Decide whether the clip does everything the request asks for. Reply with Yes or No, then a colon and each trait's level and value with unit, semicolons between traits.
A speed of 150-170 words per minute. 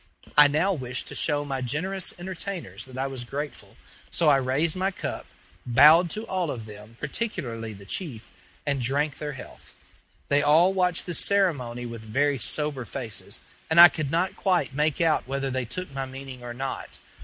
No: average, 180 wpm